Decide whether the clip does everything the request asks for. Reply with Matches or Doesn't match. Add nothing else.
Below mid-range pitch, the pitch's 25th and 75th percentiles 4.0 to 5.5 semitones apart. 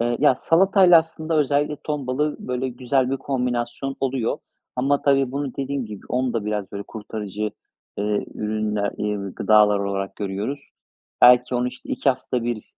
Matches